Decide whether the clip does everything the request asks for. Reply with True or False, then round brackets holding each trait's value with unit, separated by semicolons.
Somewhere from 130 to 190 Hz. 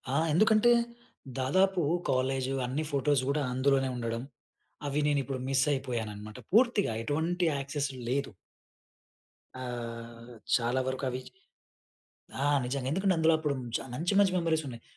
True (135 Hz)